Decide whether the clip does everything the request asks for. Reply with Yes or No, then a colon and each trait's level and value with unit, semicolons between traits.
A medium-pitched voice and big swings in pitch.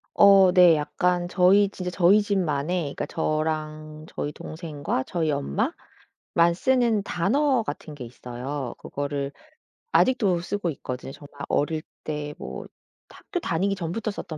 No: medium, 170 Hz; average, 4.9 semitones